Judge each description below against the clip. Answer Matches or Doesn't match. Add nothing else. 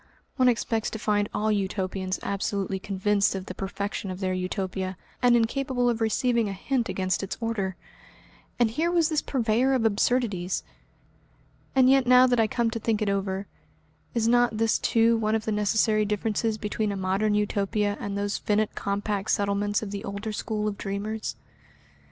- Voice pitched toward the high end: Matches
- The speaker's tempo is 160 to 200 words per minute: Matches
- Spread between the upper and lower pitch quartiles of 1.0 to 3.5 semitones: Matches